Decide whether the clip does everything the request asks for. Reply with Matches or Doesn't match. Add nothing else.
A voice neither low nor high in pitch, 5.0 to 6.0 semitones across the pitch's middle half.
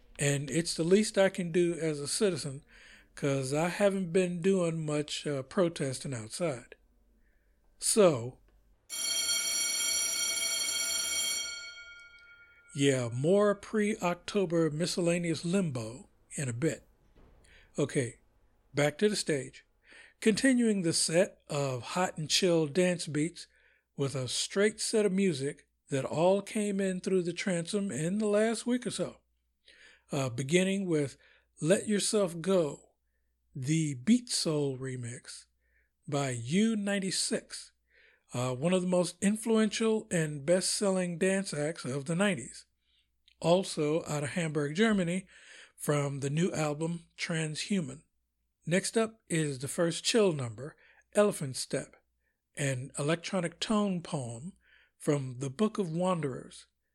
Matches